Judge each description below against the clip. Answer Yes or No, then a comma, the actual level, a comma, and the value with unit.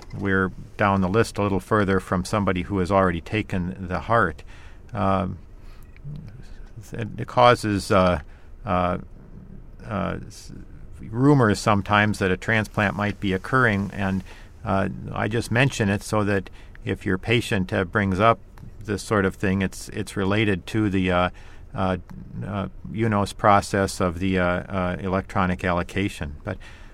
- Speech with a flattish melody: Yes, narrow, 2.3 semitones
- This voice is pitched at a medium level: No, very low, 95 Hz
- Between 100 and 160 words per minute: Yes, average, 145 wpm